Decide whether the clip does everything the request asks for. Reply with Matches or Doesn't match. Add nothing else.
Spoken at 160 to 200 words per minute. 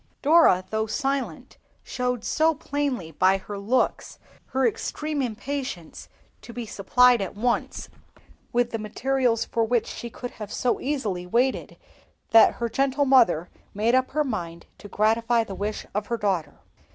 Doesn't match